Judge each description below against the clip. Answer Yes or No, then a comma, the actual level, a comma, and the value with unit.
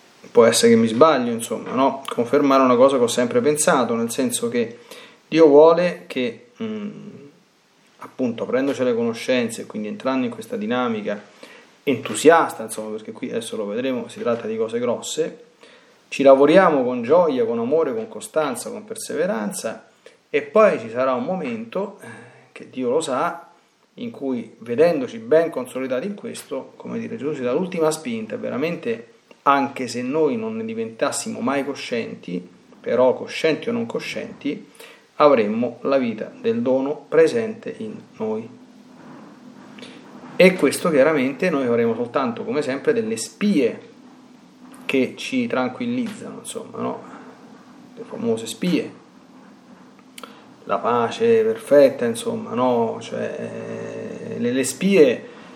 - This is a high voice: Yes, high, 230 Hz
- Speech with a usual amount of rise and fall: No, wide, 7.5 semitones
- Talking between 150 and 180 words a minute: No, average, 135 wpm